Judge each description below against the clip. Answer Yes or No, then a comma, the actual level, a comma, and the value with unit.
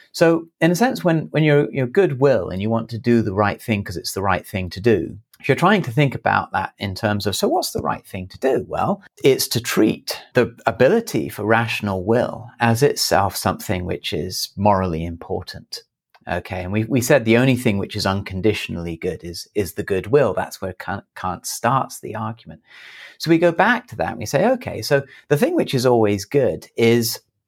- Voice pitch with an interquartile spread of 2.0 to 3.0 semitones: No, wide, 5.6 semitones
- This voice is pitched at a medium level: No, low, 115 Hz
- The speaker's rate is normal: No, fast, 215 wpm